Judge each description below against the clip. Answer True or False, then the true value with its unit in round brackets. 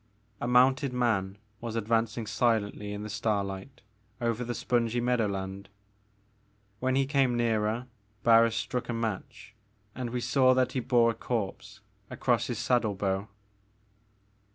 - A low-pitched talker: True (115 Hz)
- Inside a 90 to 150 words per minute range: True (135 wpm)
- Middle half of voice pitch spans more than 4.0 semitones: False (2.7 semitones)